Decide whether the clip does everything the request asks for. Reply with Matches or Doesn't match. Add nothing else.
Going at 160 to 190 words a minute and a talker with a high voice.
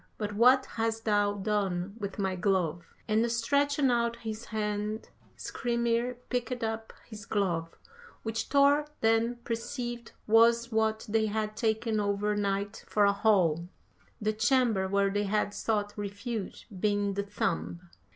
Doesn't match